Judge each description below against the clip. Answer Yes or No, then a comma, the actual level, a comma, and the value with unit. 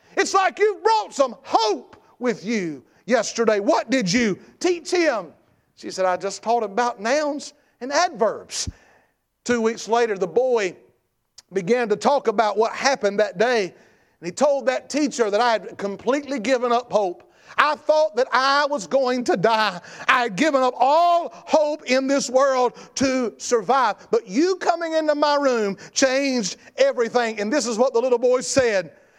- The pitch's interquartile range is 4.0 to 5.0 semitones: Yes, average, 4.6 semitones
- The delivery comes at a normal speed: Yes, average, 175 wpm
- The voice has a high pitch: Yes, very high, 250 Hz